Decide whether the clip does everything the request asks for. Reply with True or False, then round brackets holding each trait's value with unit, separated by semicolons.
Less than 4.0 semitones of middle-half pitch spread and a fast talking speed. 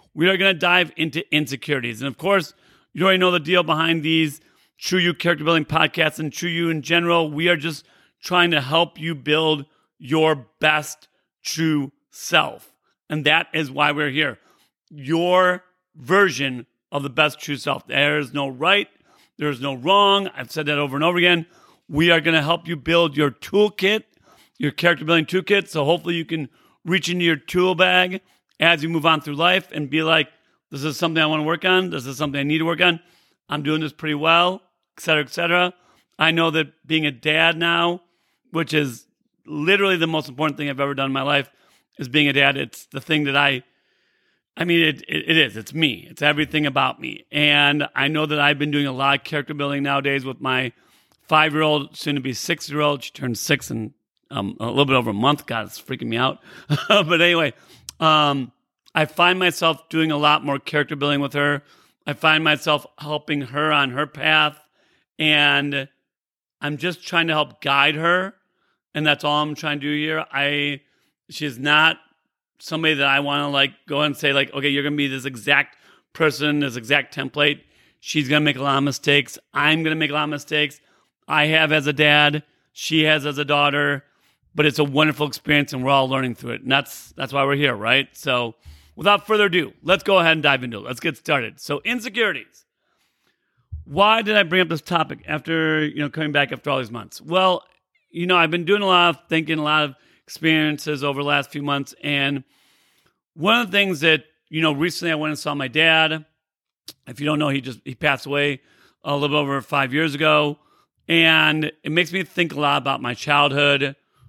True (2.6 semitones; 210 wpm)